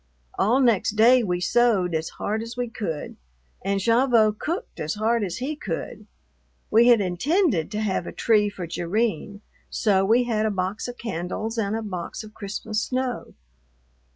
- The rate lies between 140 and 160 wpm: No, average, 170 wpm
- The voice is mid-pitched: No, high, 215 Hz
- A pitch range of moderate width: Yes, average, 3.6 semitones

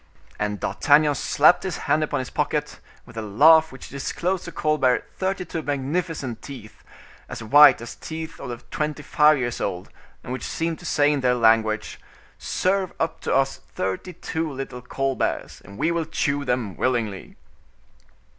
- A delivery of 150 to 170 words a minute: Yes, average, 165 wpm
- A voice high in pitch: No, medium, 140 Hz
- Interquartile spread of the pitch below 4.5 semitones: No, average, 4.8 semitones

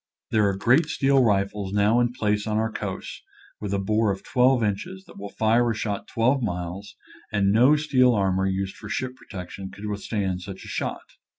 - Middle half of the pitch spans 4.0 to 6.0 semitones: No, average, 3.6 semitones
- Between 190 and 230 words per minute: Yes, average, 195 wpm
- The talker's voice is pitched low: Yes, low, 105 Hz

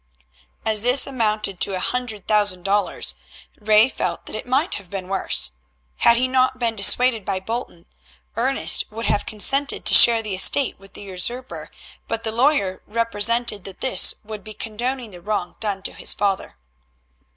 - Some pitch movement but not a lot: Yes, average, 3.6 semitones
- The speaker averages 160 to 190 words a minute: Yes, average, 170 wpm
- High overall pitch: Yes, high, 215 Hz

